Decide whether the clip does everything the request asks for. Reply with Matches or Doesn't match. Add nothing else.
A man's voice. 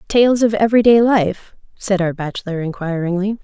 Doesn't match